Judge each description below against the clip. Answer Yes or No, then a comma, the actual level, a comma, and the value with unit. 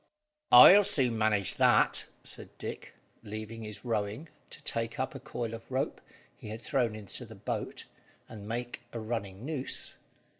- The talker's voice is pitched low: Yes, low, 115 Hz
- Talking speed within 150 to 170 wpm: Yes, average, 155 wpm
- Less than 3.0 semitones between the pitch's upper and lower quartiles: Yes, narrow, 2.5 semitones